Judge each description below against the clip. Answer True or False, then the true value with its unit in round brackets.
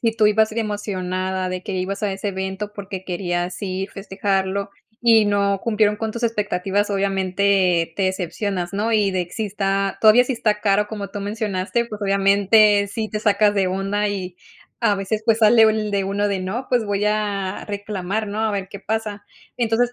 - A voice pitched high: True (200 Hz)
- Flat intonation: True (1.9 semitones)